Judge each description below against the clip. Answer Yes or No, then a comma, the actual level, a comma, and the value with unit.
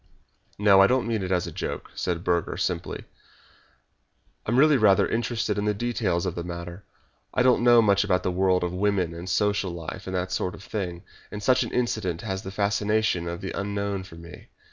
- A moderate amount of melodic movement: Yes, average, 3.0 semitones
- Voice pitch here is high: No, very low, 95 Hz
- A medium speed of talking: No, fast, 210 wpm